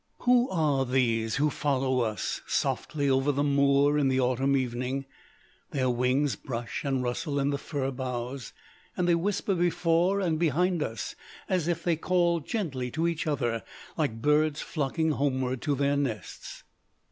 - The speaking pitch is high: No, medium, 140 Hz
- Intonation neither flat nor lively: Yes, average, 4.0 semitones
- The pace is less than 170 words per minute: Yes, average, 160 wpm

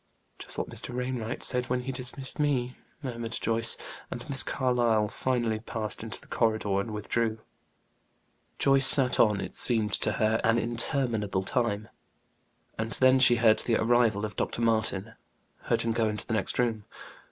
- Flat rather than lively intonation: Yes, narrow, 2.3 semitones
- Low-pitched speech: Yes, low, 115 Hz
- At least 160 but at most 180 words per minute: Yes, average, 165 wpm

